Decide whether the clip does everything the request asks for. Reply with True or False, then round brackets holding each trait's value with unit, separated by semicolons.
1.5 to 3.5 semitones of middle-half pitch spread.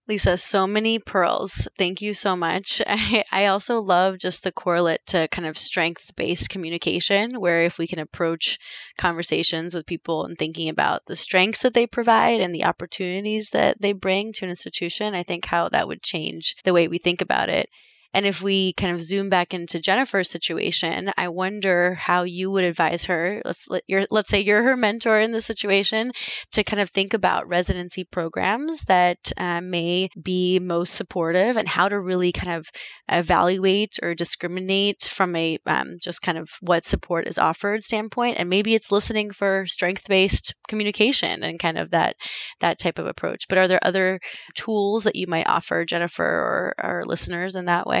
True (2.8 semitones)